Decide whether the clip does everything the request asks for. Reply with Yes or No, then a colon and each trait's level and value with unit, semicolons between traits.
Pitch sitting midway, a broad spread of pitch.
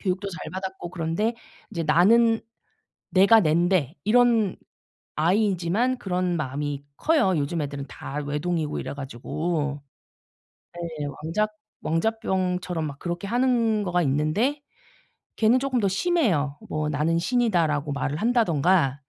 Yes: medium, 175 Hz; wide, 6.2 semitones